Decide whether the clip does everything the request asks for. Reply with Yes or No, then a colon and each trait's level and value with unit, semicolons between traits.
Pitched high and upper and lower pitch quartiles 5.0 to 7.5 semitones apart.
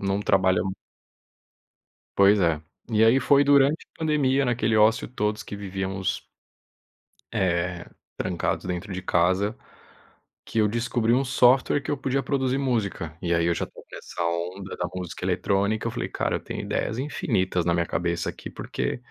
No: low, 105 Hz; average, 5.3 semitones